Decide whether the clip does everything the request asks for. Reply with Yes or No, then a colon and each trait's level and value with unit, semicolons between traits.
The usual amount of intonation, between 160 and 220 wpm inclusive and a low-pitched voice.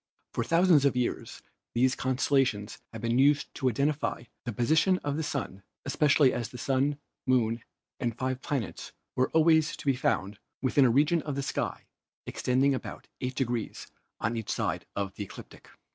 Yes: average, 3.3 semitones; average, 175 wpm; low, 130 Hz